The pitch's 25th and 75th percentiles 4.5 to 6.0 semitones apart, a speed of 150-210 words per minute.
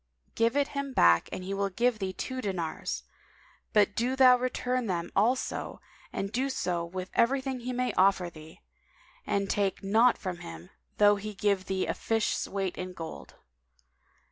Yes: average, 5.0 semitones; average, 170 wpm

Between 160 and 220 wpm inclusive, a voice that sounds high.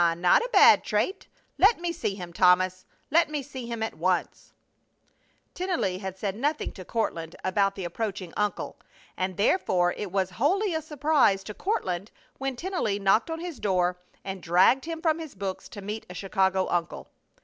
Yes: average, 180 wpm; high, 200 Hz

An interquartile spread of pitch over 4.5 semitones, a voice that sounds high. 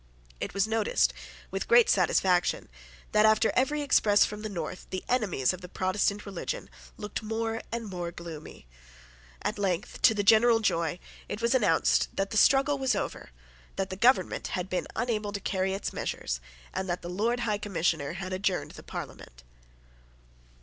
No: average, 3.6 semitones; high, 200 Hz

